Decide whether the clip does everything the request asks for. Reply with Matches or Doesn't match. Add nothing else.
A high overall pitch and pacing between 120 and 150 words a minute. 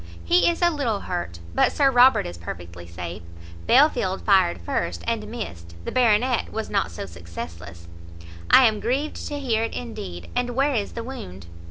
Doesn't match